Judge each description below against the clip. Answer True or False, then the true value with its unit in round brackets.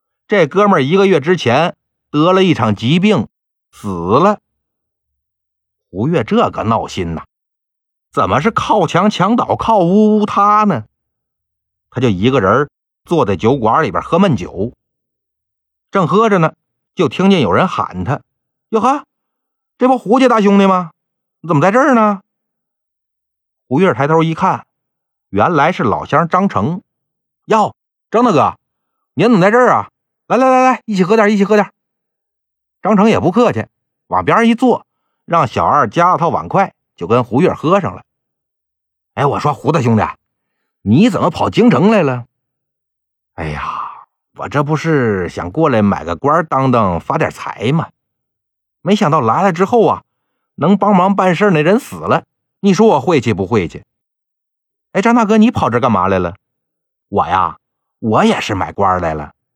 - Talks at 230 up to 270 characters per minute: False (220 characters per minute)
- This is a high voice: False (180 Hz)